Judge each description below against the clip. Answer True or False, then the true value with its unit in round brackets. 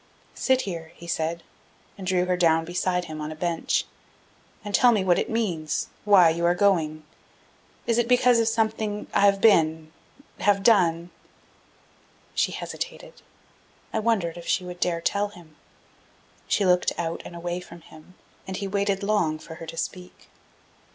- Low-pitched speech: False (180 Hz)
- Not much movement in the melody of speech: False (3.6 semitones)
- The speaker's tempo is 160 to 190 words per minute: True (170 wpm)